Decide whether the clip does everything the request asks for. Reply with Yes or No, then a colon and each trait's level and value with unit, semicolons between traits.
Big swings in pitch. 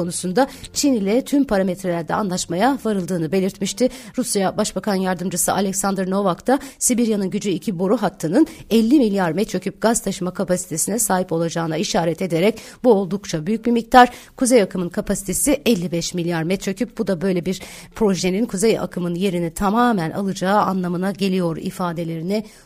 No: average, 3.7 semitones